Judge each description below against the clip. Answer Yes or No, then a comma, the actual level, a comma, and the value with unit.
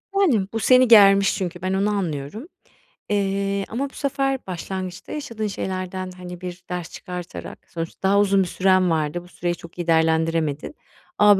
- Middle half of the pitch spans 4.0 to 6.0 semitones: No, average, 2.8 semitones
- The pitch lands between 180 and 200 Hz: Yes, medium, 185 Hz